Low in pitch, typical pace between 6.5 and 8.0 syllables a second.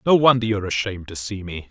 Yes: low, 105 Hz; 7.6 syllables/s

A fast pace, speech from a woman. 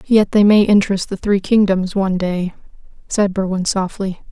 No: average, 165 wpm; female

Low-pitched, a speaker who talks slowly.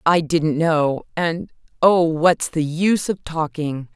No: medium, 160 Hz; slow, 120 wpm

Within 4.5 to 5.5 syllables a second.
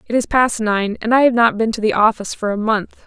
No: 5.8 syllables/s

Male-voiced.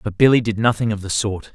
Yes: male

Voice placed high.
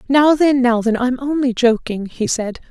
Yes: very high, 250 Hz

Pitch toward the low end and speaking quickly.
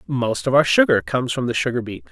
Yes: low, 125 Hz; fast, 255 wpm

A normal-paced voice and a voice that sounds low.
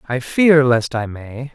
Yes: average, 195 wpm; low, 130 Hz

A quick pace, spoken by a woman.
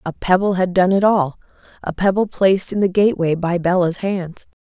No: average, 180 wpm; female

